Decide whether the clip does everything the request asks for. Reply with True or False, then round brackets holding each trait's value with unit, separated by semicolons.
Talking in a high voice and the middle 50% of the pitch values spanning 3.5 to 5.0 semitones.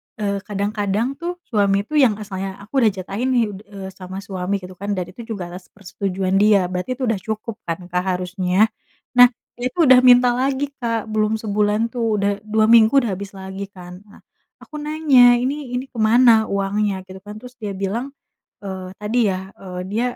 True (210 Hz; 3.8 semitones)